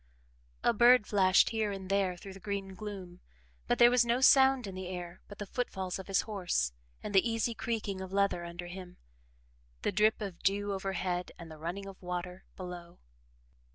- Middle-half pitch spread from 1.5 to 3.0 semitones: Yes, narrow, 2.6 semitones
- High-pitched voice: Yes, high, 195 Hz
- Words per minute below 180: No, average, 190 wpm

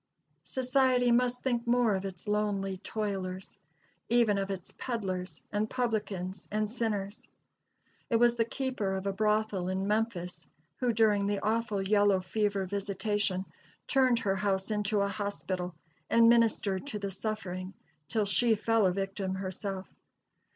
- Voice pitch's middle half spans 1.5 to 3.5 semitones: Yes, average, 2.8 semitones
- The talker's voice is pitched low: No, high, 205 Hz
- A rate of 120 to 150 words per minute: Yes, average, 145 wpm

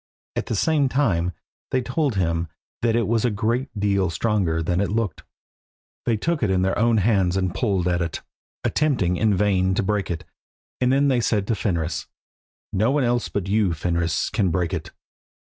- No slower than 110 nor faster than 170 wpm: No, average, 190 wpm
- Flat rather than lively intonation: No, average, 4.6 semitones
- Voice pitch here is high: No, low, 100 Hz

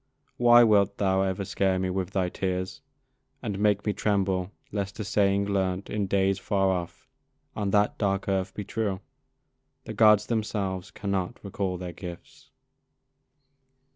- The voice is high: No, low, 100 Hz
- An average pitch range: No, narrow, 1.6 semitones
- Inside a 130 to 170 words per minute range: Yes, average, 145 wpm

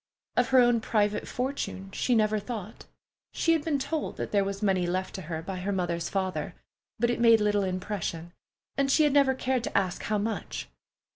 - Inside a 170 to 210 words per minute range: Yes, average, 200 wpm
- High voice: Yes, high, 210 Hz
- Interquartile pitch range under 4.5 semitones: No, average, 4.8 semitones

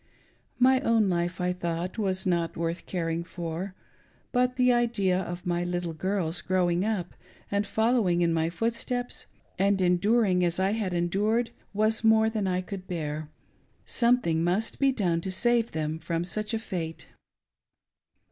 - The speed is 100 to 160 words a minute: Yes, average, 155 wpm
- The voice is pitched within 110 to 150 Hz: No, medium, 185 Hz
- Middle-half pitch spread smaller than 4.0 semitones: No, average, 4.3 semitones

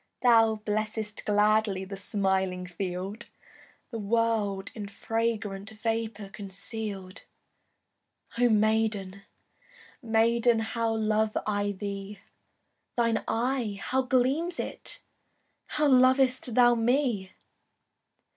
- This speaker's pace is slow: Yes, slow, 90 wpm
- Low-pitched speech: No, high, 220 Hz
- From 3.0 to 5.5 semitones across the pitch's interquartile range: No, narrow, 2.5 semitones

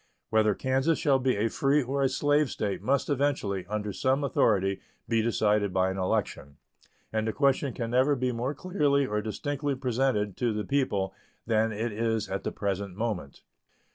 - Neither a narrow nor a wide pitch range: Yes, average, 4.7 semitones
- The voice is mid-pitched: No, low, 115 Hz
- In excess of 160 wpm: Yes, average, 175 wpm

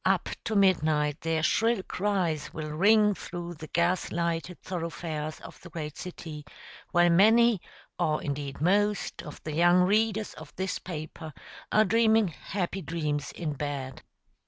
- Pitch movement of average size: Yes, average, 4.3 semitones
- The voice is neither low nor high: Yes, medium, 170 Hz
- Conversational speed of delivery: Yes, average, 145 wpm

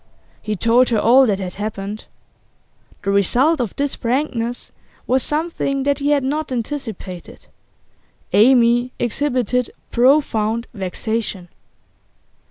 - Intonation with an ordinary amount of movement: Yes, average, 4.1 semitones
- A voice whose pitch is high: Yes, high, 240 Hz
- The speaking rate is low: Yes, slow, 110 wpm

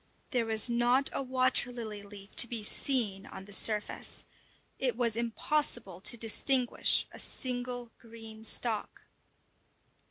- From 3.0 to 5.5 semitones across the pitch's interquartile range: No, narrow, 2.6 semitones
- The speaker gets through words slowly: Yes, slow, 130 wpm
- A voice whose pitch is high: Yes, high, 235 Hz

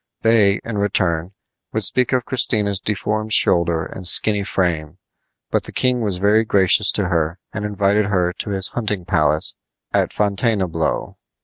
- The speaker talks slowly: No, average, 150 wpm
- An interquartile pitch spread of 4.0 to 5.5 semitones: No, average, 3.2 semitones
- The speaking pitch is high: No, low, 100 Hz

